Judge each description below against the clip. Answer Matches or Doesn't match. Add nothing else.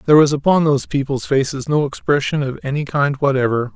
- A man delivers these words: Matches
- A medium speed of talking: Matches